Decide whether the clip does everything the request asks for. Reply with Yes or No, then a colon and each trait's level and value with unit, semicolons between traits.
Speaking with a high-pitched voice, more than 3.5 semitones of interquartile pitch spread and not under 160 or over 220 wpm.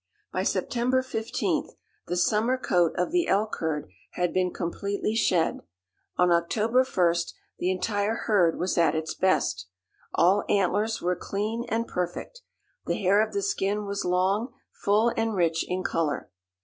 No: high, 195 Hz; average, 4.1 semitones; average, 150 wpm